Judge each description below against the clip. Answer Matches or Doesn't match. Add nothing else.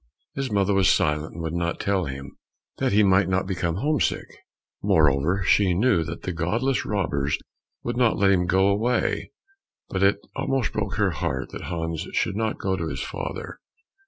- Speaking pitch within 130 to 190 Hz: Doesn't match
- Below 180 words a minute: Doesn't match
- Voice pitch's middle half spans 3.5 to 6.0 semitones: Matches